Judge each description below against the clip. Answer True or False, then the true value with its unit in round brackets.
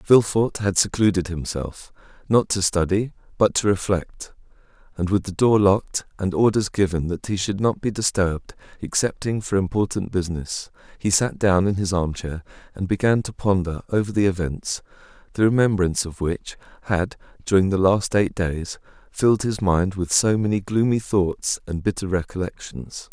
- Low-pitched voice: True (95 Hz)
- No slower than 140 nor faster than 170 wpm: True (165 wpm)